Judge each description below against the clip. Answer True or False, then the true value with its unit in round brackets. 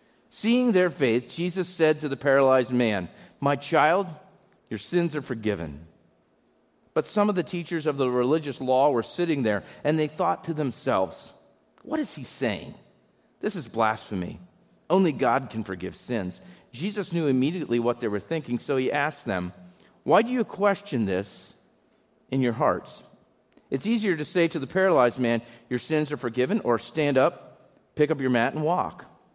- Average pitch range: False (6.3 semitones)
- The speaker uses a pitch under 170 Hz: True (140 Hz)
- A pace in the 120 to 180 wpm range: True (170 wpm)